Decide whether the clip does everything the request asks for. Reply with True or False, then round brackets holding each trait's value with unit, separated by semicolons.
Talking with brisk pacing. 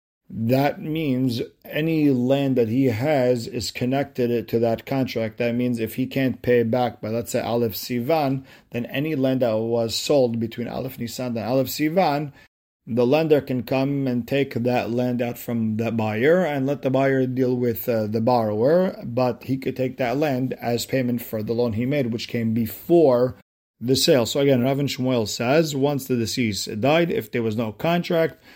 False (185 wpm)